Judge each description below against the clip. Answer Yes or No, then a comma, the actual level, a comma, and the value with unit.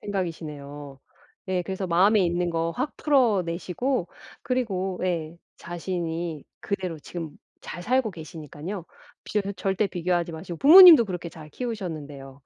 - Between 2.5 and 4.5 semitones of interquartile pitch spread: Yes, average, 3.6 semitones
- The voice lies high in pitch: No, medium, 180 Hz